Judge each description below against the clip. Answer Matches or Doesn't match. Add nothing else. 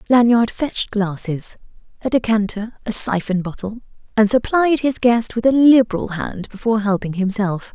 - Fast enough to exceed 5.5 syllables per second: Doesn't match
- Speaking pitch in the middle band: Doesn't match